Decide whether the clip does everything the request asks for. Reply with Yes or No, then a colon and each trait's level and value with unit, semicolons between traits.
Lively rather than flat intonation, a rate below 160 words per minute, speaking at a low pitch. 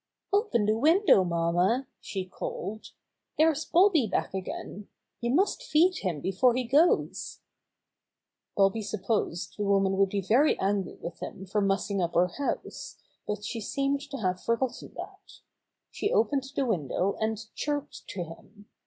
No: wide, 6.2 semitones; average, 150 wpm; high, 215 Hz